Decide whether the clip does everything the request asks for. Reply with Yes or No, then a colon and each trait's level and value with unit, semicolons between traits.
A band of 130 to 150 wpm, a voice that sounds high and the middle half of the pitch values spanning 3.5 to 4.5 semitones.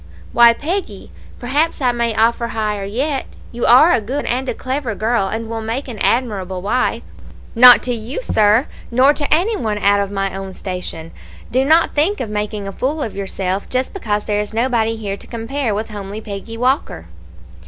No: average, 190 wpm; high, 230 Hz; average, 3.9 semitones